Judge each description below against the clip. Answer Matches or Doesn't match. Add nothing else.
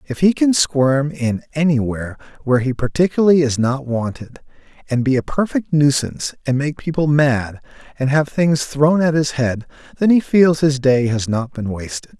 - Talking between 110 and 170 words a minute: Doesn't match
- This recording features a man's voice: Matches